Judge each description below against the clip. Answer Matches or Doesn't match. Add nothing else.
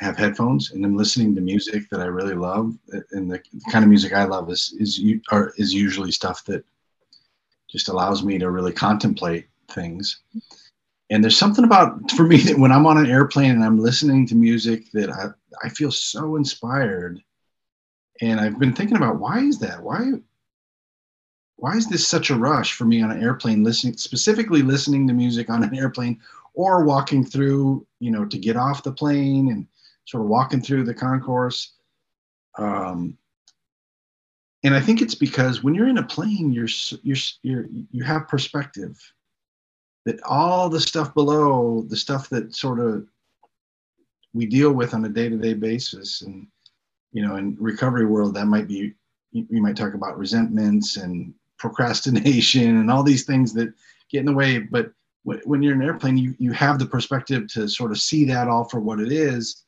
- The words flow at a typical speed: Matches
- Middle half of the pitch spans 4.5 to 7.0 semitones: Matches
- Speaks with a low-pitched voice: Matches